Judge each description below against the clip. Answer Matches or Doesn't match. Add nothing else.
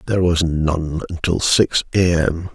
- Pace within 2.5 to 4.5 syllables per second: Matches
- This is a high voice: Doesn't match